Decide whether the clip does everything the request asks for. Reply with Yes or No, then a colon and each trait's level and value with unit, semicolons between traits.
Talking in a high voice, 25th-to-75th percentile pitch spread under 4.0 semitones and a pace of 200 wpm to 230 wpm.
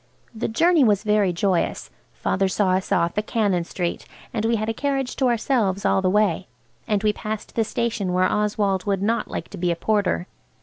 Yes: high, 210 Hz; average, 3.1 semitones; fast, 205 wpm